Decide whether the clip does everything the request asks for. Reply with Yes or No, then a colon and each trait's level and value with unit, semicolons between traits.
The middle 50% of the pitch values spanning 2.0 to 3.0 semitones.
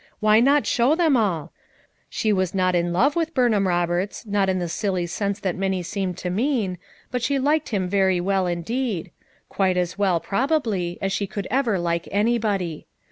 No: average, 4.6 semitones